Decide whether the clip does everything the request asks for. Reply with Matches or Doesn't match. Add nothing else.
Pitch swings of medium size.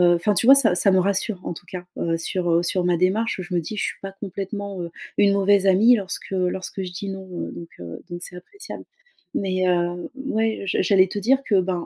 Doesn't match